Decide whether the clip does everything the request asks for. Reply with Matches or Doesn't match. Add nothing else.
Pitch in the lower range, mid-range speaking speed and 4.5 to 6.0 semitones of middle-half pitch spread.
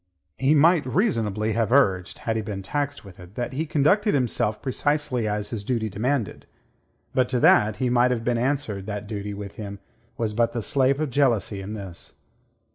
Matches